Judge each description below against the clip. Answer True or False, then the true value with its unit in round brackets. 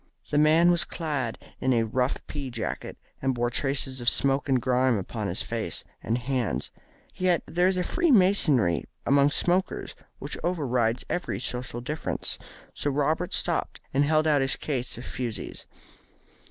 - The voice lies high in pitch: False (135 Hz)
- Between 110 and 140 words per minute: False (155 wpm)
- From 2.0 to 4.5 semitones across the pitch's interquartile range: True (4.2 semitones)